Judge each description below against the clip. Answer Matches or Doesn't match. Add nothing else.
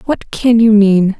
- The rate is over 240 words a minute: Doesn't match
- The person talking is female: Matches